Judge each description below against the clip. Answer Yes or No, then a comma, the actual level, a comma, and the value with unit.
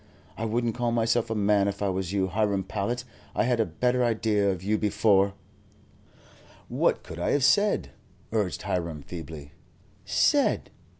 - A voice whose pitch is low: Yes, low, 105 Hz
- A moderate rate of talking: Yes, average, 160 wpm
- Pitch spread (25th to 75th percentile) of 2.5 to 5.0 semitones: Yes, average, 3.4 semitones